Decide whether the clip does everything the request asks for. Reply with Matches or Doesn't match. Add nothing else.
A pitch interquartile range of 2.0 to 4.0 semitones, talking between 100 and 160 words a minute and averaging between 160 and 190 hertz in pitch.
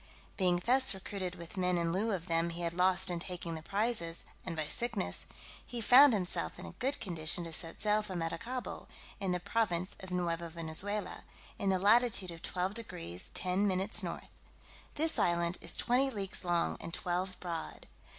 Doesn't match